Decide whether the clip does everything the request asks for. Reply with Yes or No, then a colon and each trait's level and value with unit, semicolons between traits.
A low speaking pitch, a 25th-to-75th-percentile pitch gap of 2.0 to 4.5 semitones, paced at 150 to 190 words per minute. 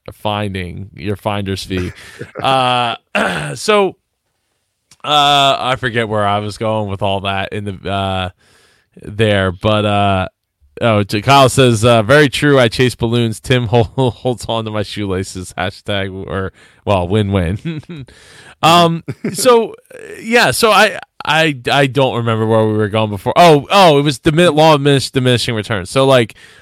No: low, 115 Hz; wide, 5.4 semitones; average, 155 wpm